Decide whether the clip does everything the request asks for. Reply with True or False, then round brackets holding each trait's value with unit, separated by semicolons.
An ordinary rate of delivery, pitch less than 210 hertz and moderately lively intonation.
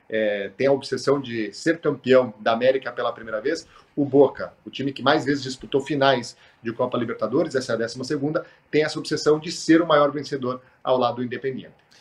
False (205 wpm; 135 Hz; 3.1 semitones)